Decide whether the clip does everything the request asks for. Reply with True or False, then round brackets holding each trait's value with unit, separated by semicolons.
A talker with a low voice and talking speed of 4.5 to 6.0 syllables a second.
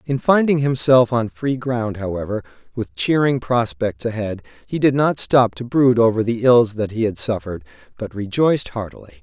True (115 Hz; 5.0 syllables/s)